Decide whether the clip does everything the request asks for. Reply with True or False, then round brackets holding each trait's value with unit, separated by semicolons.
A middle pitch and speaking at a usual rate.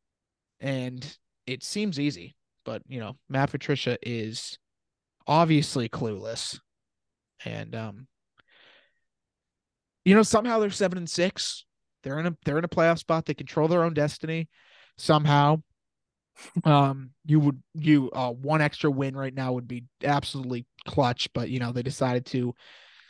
True (145 Hz; 145 wpm)